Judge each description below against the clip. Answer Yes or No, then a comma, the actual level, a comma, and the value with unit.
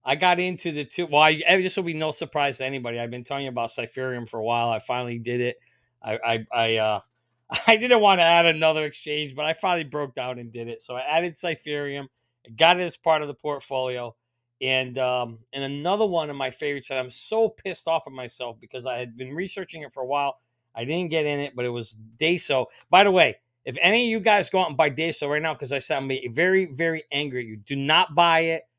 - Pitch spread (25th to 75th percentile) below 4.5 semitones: No, average, 4.9 semitones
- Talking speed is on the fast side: Yes, fast, 245 wpm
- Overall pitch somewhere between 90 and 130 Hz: No, medium, 140 Hz